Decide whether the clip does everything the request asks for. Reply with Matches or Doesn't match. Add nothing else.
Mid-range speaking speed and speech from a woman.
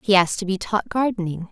Doesn't match